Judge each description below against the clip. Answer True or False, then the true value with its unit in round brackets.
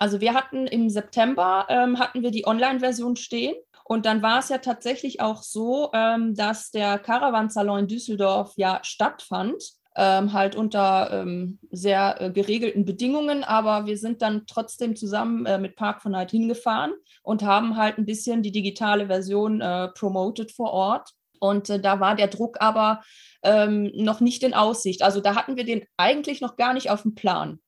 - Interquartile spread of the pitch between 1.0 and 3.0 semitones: True (2.7 semitones)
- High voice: True (215 Hz)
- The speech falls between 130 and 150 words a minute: False (185 wpm)